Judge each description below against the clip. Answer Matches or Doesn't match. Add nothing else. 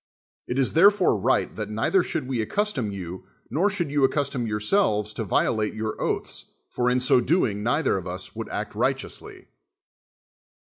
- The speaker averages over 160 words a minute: Matches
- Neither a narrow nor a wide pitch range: Doesn't match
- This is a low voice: Matches